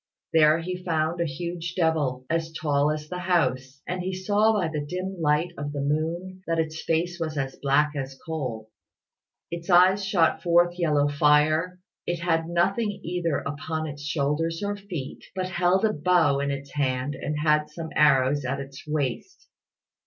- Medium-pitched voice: Yes, medium, 160 Hz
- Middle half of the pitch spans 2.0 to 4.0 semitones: Yes, average, 3.3 semitones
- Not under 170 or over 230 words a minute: Yes, average, 175 wpm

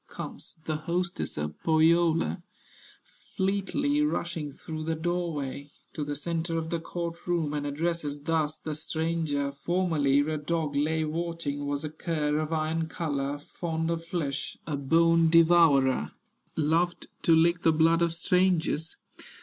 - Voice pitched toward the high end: No, medium, 160 Hz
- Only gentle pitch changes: Yes, narrow, 2.3 semitones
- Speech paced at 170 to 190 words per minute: No, average, 145 wpm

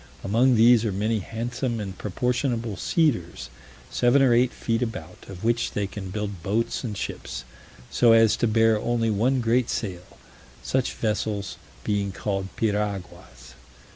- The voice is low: Yes, low, 110 Hz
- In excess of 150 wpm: No, average, 145 wpm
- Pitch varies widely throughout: No, average, 3.1 semitones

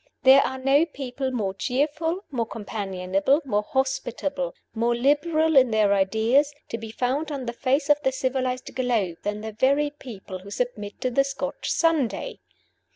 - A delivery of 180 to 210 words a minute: No, average, 160 wpm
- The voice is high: Yes, very high, 255 Hz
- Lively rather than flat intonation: No, average, 4.5 semitones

